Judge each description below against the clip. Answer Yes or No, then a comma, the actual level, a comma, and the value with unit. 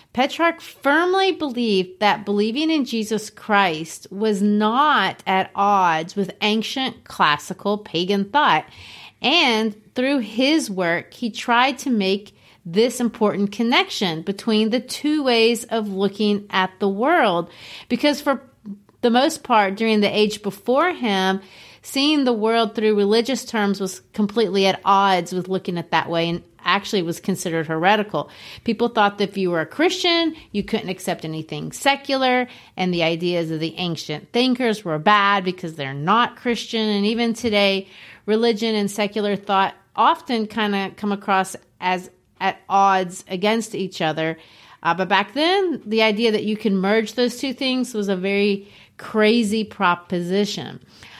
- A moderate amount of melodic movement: Yes, average, 3.7 semitones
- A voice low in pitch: No, high, 210 Hz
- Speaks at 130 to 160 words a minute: Yes, average, 150 wpm